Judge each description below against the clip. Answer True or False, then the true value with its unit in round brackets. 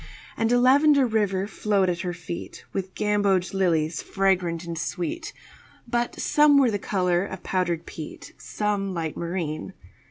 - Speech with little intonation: False (3.4 semitones)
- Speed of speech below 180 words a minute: True (150 wpm)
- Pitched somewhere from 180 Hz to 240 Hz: True (190 Hz)